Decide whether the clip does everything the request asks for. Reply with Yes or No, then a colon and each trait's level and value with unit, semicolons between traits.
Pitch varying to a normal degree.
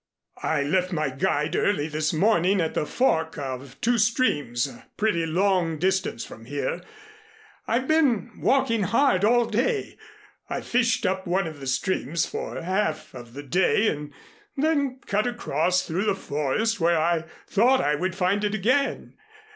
No: wide, 6.6 semitones